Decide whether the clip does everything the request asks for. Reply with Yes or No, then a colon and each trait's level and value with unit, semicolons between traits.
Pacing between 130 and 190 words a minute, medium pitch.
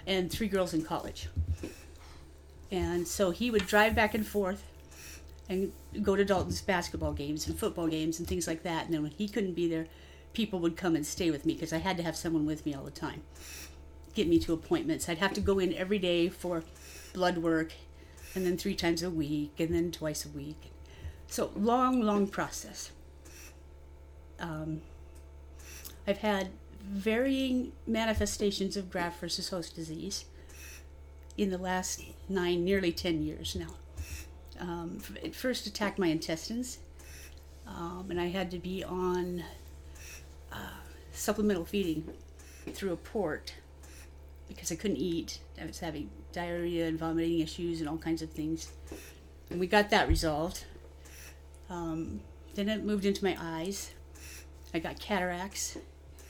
Yes: average, 160 wpm; medium, 160 Hz